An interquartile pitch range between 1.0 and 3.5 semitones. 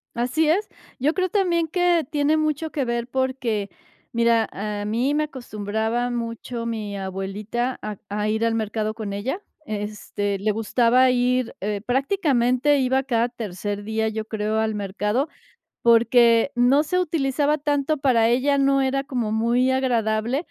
No: average, 4.1 semitones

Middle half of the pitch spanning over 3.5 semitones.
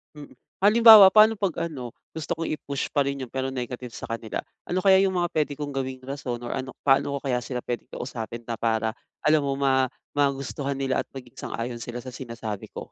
No: average, 3.2 semitones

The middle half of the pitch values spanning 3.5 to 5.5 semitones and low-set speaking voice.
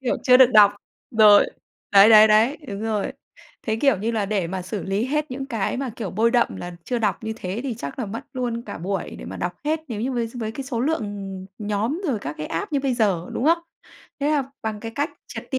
No: average, 4.2 semitones; high, 225 Hz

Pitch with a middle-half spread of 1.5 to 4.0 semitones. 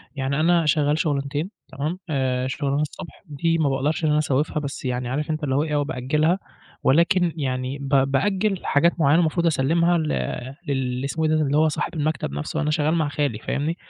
Yes: average, 2.7 semitones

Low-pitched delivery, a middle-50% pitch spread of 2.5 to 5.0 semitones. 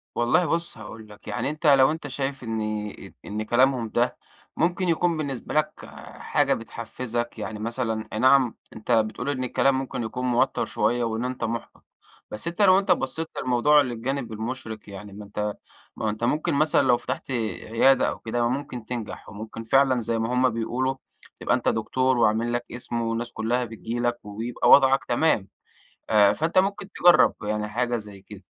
Yes: low, 120 Hz; average, 3.4 semitones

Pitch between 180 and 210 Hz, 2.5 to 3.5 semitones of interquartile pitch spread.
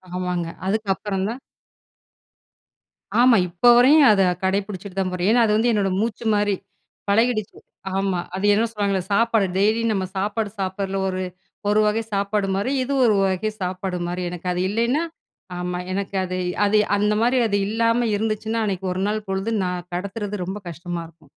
Yes: high, 200 Hz; average, 2.8 semitones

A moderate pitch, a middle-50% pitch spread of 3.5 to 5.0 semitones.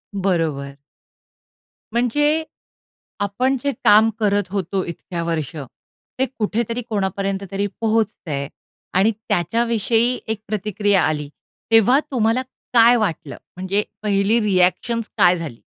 No: high, 205 Hz; average, 3.9 semitones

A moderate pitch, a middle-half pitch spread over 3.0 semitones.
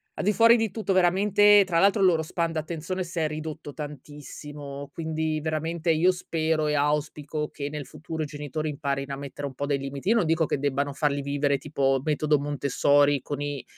No: medium, 150 Hz; narrow, 2.5 semitones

